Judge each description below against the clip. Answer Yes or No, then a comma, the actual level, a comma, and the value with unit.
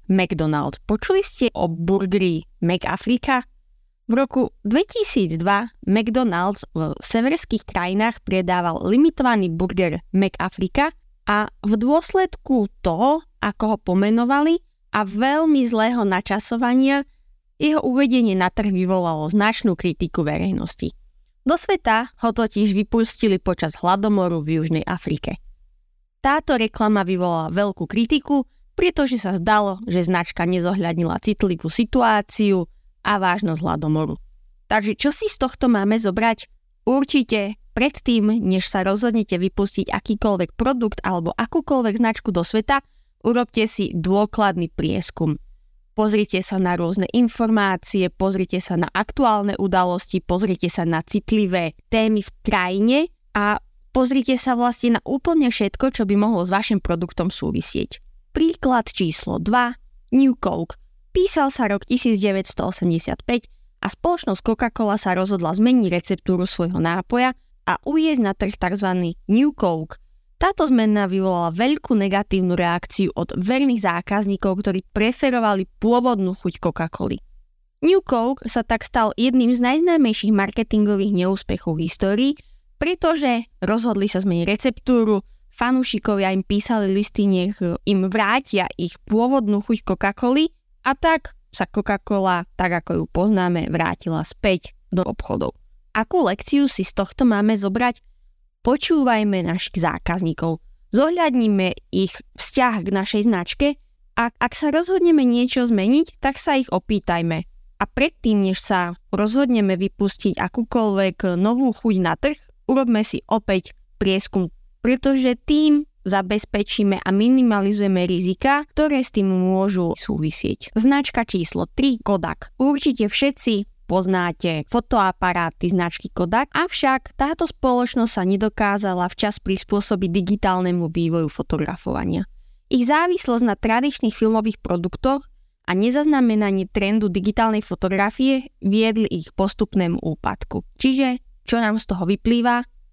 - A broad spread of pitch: No, average, 4.8 semitones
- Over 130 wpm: No, average, 120 wpm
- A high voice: Yes, high, 210 Hz